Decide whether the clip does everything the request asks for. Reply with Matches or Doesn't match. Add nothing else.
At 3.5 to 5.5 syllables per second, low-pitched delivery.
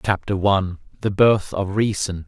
Matches